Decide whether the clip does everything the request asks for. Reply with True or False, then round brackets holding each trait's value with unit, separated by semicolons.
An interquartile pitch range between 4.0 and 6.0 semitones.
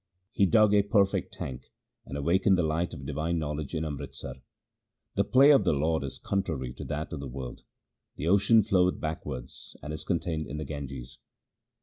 True (5.2 semitones)